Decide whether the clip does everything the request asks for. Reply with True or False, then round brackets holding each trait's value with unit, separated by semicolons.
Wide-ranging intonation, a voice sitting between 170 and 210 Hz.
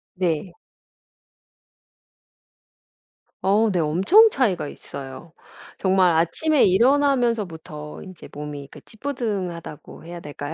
True (6.4 semitones; 185 Hz)